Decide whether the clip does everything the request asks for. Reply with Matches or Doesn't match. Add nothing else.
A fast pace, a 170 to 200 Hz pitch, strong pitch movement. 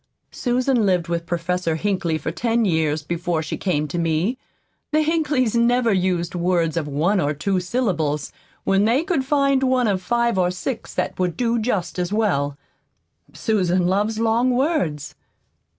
Doesn't match